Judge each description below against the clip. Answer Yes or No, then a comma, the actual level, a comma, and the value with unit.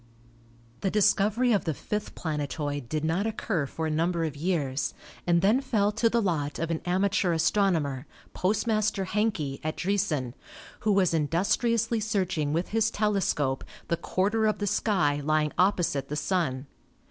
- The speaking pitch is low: No, medium, 180 Hz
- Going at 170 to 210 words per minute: No, average, 160 wpm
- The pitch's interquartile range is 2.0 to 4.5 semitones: No, wide, 5.4 semitones